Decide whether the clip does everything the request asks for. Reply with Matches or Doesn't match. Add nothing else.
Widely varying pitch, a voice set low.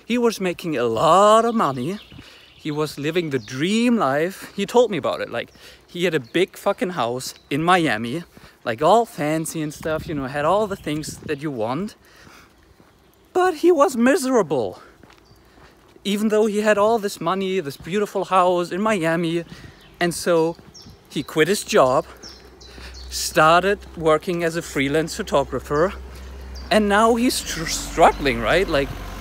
Doesn't match